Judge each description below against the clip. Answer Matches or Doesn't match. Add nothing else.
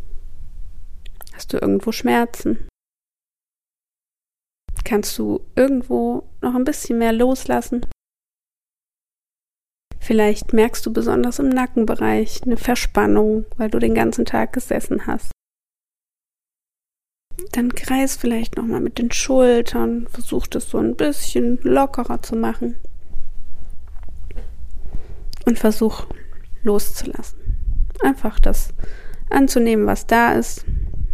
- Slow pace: Matches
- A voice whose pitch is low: Doesn't match